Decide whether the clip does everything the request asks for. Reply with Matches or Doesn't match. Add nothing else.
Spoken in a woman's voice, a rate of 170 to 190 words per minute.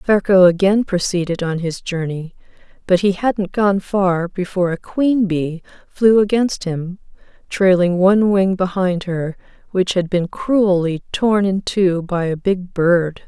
Doesn't match